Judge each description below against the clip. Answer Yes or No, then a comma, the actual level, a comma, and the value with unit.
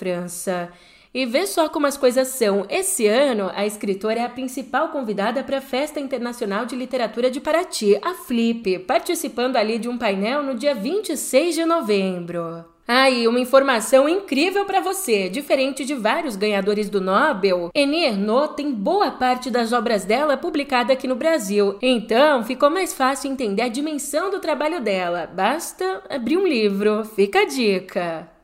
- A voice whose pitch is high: Yes, very high, 255 Hz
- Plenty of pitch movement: Yes, wide, 5.7 semitones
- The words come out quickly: No, average, 160 wpm